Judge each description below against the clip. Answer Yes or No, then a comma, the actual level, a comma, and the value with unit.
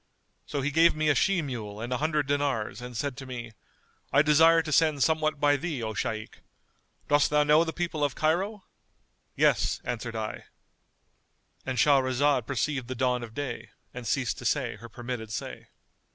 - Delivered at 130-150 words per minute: No, average, 175 wpm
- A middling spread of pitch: Yes, average, 4.0 semitones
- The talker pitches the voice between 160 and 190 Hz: No, medium, 140 Hz